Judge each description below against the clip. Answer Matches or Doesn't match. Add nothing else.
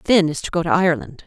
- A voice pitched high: Doesn't match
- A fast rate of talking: Matches